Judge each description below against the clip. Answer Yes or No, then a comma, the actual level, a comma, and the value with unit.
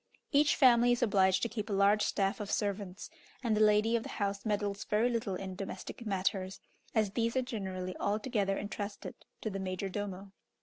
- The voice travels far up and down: No, narrow, 2.4 semitones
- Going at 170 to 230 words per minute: Yes, average, 185 wpm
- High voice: Yes, high, 205 Hz